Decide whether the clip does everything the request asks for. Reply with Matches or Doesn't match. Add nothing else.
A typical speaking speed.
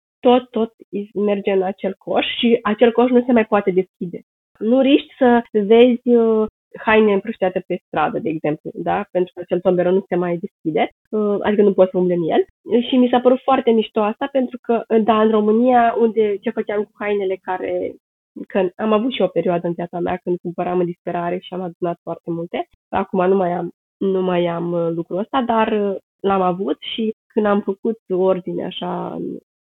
Doesn't match